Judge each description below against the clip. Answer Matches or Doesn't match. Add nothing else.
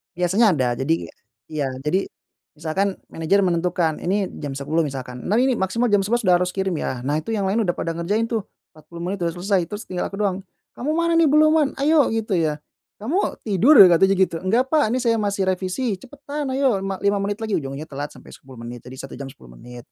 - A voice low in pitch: Doesn't match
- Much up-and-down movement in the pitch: Matches